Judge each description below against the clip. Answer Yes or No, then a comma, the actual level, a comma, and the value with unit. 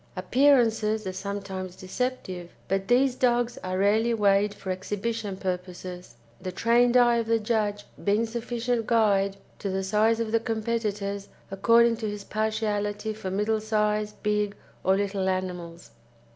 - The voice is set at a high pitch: Yes, high, 210 Hz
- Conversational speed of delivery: Yes, average, 145 wpm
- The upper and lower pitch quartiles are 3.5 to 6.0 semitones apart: No, average, 2.8 semitones